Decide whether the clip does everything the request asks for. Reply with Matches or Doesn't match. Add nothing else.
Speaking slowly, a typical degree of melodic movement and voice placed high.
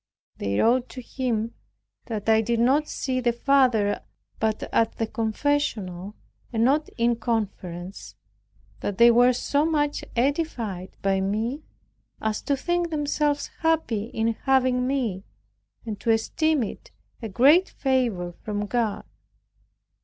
Matches